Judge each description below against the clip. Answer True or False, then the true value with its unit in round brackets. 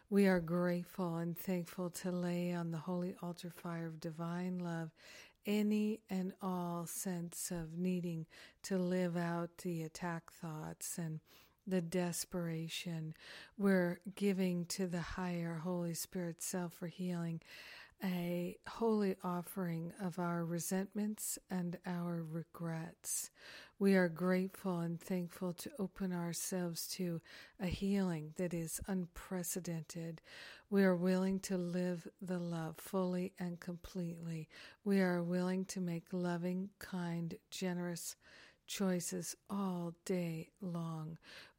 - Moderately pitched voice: True (180 Hz)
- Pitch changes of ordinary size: False (1.7 semitones)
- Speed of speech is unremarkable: False (125 wpm)